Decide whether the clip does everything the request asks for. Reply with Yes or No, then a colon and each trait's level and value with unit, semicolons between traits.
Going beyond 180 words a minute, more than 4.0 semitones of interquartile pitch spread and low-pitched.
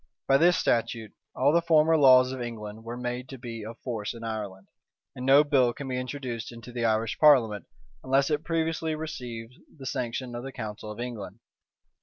No: average, 190 wpm; average, 3.3 semitones; low, 125 Hz